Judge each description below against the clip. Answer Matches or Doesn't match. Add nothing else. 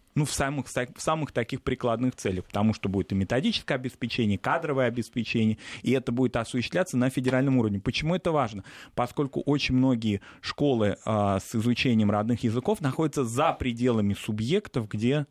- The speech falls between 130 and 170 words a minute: Matches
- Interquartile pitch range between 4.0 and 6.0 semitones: Doesn't match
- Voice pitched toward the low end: Matches